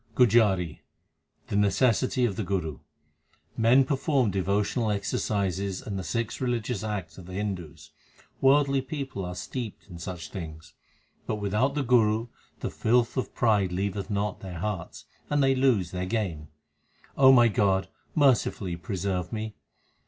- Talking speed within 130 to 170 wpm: Yes, average, 145 wpm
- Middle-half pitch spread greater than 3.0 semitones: Yes, average, 4.7 semitones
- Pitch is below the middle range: Yes, low, 105 Hz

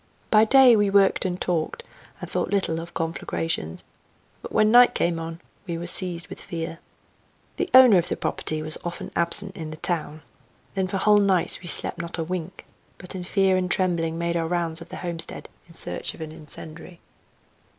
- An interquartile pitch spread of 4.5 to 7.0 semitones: No, average, 2.7 semitones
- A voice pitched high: No, medium, 175 Hz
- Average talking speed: Yes, average, 190 wpm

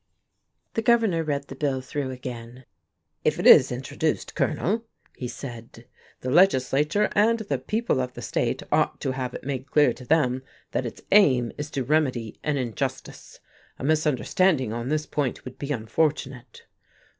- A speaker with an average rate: Yes, average, 160 wpm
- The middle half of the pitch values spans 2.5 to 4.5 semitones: Yes, average, 3.7 semitones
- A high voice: No, medium, 140 Hz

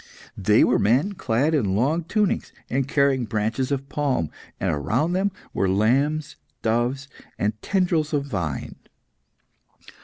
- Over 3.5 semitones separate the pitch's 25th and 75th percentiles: Yes, wide, 5.6 semitones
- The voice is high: No, low, 135 Hz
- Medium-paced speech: No, slow, 130 wpm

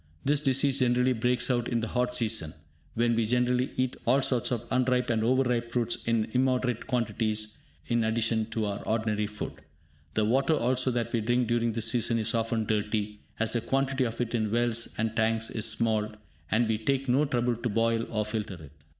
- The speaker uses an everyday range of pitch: No, narrow, 2.0 semitones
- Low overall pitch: Yes, low, 115 Hz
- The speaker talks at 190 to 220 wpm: Yes, average, 200 wpm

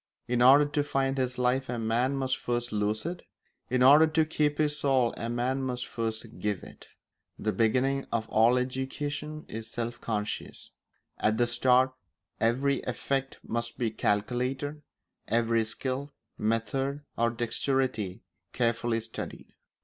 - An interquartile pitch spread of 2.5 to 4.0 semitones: Yes, average, 2.9 semitones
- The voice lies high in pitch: No, low, 125 Hz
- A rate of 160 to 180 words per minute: No, average, 140 wpm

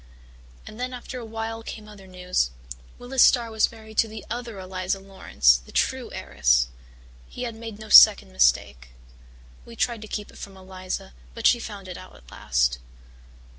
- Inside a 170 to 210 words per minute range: Yes, average, 175 wpm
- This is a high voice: Yes, high, 205 Hz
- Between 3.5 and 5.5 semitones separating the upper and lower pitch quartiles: Yes, average, 3.9 semitones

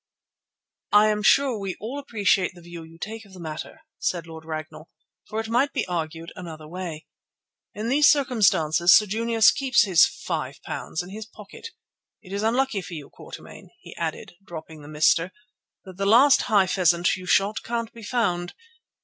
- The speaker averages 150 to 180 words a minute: Yes, average, 175 wpm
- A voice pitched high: Yes, high, 195 Hz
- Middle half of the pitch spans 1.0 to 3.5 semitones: No, average, 4.9 semitones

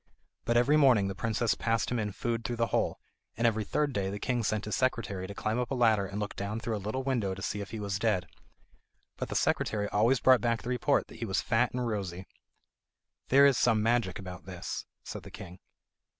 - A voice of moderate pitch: No, low, 110 Hz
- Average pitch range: Yes, average, 3.3 semitones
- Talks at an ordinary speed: No, fast, 230 wpm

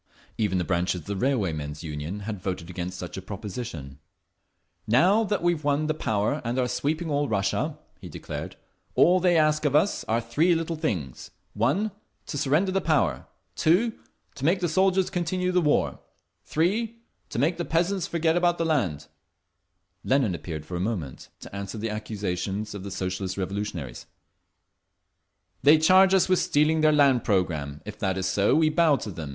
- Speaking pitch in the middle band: No, low, 125 Hz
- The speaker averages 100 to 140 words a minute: No, average, 175 wpm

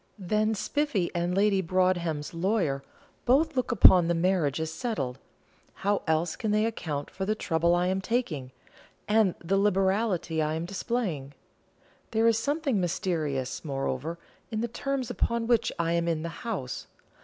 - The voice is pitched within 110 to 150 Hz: No, medium, 185 Hz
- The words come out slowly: No, average, 155 wpm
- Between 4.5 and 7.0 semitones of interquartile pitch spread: Yes, average, 5.2 semitones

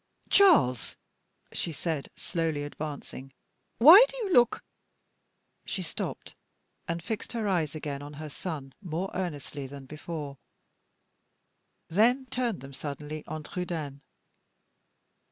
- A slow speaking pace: Yes, slow, 120 wpm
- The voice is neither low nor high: Yes, medium, 155 Hz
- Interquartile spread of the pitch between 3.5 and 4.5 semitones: No, average, 5.0 semitones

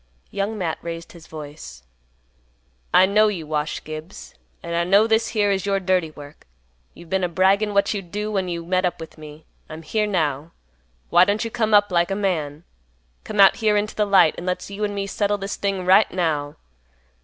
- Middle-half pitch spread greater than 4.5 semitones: No, average, 3.8 semitones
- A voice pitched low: No, medium, 185 Hz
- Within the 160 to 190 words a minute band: No, fast, 205 wpm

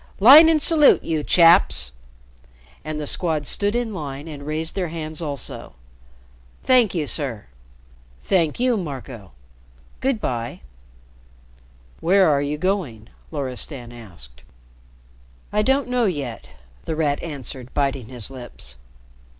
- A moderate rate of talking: No, slow, 125 wpm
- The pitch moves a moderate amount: No, wide, 6.7 semitones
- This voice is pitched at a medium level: Yes, medium, 150 Hz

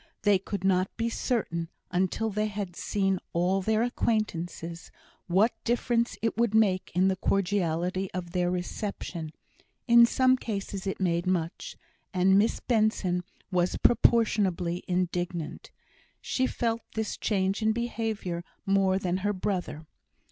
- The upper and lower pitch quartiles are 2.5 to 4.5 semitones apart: Yes, average, 3.5 semitones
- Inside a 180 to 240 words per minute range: No, slow, 135 wpm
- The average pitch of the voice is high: Yes, high, 195 Hz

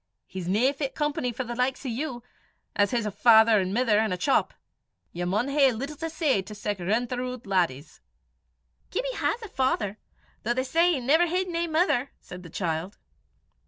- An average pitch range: No, wide, 5.7 semitones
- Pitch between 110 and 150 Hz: No, high, 245 Hz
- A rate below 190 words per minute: No, average, 195 wpm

